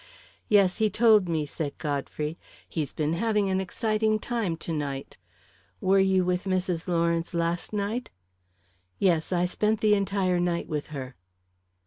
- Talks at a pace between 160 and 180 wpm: No, average, 145 wpm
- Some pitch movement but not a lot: Yes, average, 3.8 semitones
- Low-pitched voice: No, medium, 180 Hz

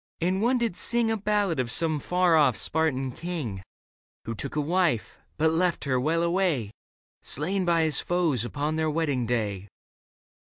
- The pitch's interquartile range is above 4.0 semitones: Yes, wide, 5.4 semitones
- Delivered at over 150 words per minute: Yes, average, 165 wpm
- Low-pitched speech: No, medium, 160 Hz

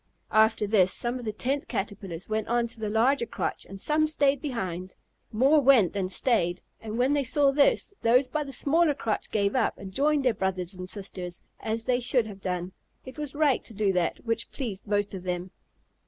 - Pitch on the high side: Yes, high, 225 Hz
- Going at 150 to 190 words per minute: No, fast, 205 wpm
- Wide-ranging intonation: Yes, wide, 5.7 semitones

